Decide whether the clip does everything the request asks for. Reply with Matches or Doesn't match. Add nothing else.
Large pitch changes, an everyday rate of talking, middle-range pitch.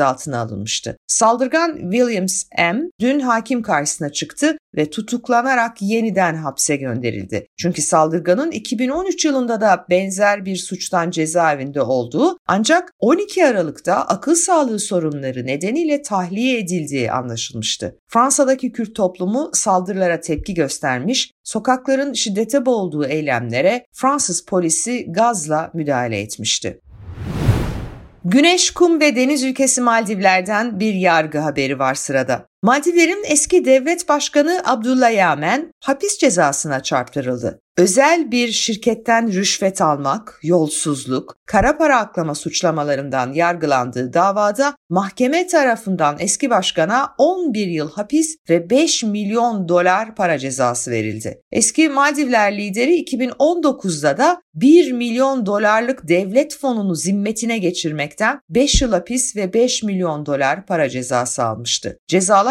Doesn't match